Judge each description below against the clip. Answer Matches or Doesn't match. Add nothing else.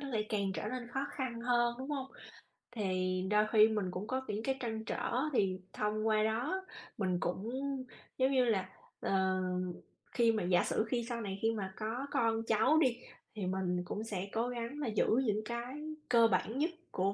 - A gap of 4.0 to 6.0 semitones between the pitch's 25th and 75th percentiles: Doesn't match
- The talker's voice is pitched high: Matches